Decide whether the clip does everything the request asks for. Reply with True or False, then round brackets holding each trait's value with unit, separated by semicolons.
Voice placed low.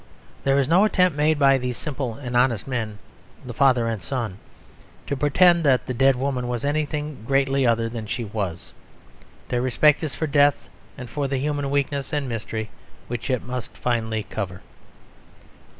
True (130 Hz)